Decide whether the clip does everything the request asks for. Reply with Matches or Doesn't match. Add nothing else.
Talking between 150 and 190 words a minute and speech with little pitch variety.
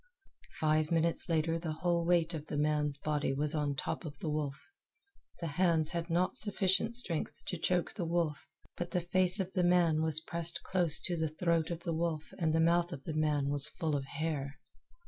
Doesn't match